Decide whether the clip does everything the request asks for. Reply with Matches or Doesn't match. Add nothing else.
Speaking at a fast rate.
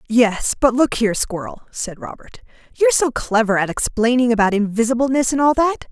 Doesn't match